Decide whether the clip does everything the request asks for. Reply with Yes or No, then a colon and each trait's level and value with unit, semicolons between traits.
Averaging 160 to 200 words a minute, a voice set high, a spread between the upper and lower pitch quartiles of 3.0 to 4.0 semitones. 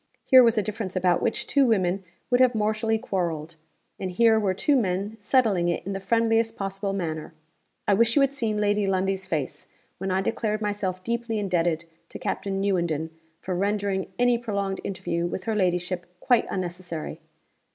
Yes: average, 170 wpm; high, 195 Hz; average, 3.4 semitones